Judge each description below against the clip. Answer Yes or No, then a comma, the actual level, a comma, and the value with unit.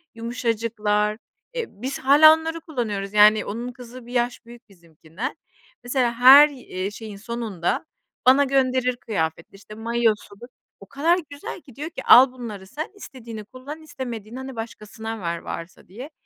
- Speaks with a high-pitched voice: Yes, high, 235 Hz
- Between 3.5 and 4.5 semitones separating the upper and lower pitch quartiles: Yes, average, 3.9 semitones